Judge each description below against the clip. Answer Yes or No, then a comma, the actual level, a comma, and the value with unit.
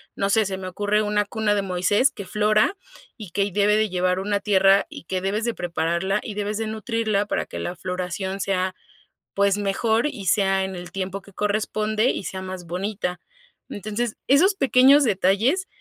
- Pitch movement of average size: No, narrow, 2.3 semitones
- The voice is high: Yes, high, 200 Hz